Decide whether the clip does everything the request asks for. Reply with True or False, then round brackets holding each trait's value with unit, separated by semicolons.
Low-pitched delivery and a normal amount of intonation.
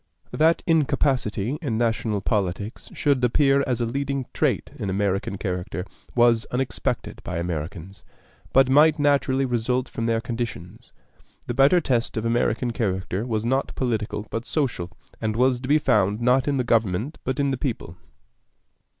True (120 Hz; 4.1 semitones)